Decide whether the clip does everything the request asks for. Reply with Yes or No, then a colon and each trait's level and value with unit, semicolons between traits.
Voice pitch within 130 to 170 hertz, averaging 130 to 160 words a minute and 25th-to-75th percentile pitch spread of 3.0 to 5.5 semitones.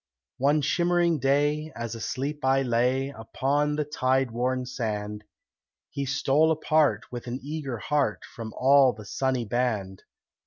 Yes: low, 135 Hz; average, 140 wpm; average, 3.6 semitones